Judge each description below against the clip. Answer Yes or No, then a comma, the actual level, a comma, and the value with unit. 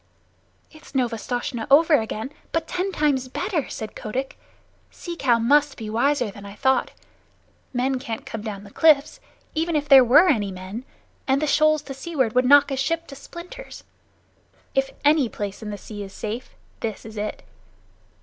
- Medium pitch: No, very high, 265 Hz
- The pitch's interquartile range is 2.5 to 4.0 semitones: No, average, 5.1 semitones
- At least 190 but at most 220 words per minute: No, average, 170 wpm